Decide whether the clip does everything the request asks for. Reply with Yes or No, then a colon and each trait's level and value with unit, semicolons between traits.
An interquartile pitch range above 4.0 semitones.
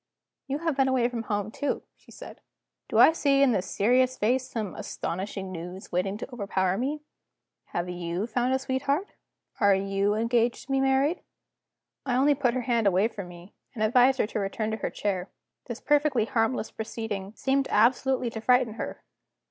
Yes: average, 4.7 semitones